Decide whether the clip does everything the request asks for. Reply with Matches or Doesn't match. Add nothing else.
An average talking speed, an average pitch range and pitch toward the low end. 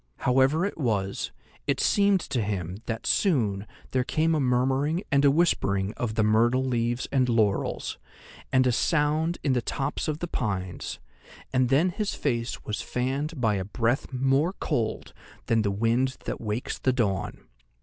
Matches